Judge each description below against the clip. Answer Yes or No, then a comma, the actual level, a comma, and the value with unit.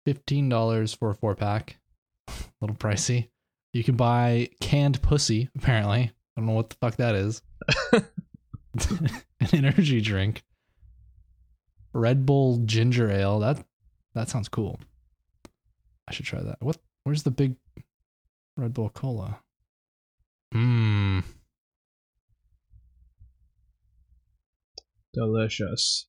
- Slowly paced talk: Yes, slow, 110 wpm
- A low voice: Yes, low, 110 Hz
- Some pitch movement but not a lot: Yes, average, 4.2 semitones